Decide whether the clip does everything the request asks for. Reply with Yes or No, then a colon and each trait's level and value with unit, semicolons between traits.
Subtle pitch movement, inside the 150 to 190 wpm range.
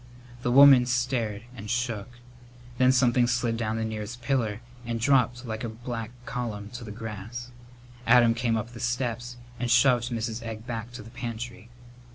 Yes: narrow, 1.7 semitones; average, 170 wpm